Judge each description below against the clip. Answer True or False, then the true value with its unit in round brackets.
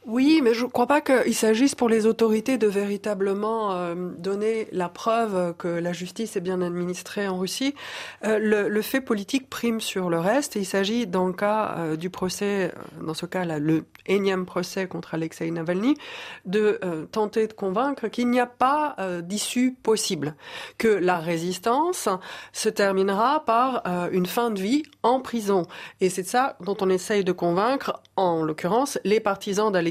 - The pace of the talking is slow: False (185 wpm)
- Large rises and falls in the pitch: False (4.2 semitones)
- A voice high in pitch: True (205 Hz)